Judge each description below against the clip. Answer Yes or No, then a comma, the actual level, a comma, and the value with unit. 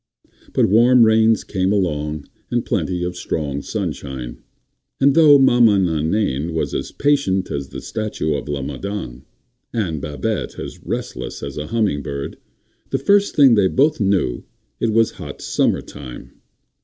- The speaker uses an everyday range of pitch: No, wide, 7.7 semitones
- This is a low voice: Yes, very low, 95 Hz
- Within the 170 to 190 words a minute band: No, average, 150 wpm